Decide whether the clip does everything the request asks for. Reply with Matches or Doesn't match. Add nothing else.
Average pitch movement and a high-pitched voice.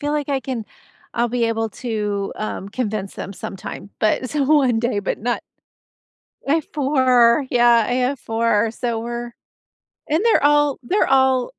Matches